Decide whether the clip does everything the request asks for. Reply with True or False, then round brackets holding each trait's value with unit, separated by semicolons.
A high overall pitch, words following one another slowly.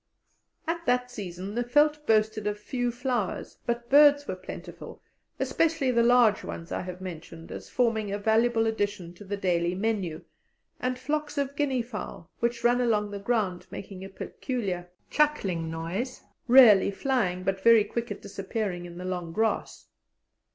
False (220 Hz; 160 wpm)